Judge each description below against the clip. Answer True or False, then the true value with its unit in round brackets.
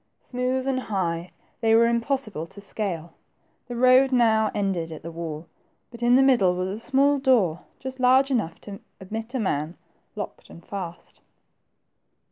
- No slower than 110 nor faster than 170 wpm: True (160 wpm)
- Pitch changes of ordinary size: False (6.1 semitones)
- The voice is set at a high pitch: True (220 Hz)